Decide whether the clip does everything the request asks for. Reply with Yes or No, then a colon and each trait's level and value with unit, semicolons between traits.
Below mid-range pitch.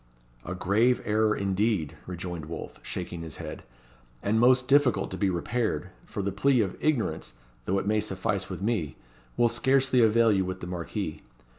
Yes: low, 105 Hz